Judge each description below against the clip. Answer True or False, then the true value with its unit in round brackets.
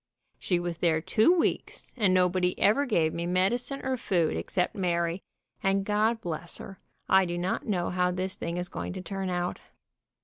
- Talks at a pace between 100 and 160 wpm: False (180 wpm)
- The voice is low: False (185 Hz)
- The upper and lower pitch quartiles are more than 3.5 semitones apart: False (2.4 semitones)